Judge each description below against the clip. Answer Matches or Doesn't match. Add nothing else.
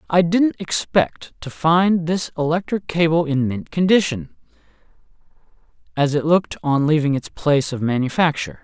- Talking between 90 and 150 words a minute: Matches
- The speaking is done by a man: Matches